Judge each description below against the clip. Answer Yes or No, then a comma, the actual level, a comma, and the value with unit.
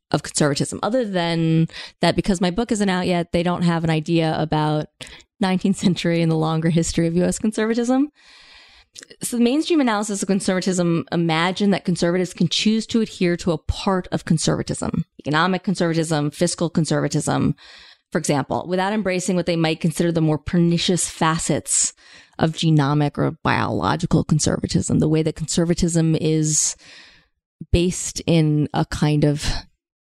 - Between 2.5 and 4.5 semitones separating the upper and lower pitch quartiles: Yes, average, 2.9 semitones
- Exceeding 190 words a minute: No, average, 150 wpm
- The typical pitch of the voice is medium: Yes, medium, 170 Hz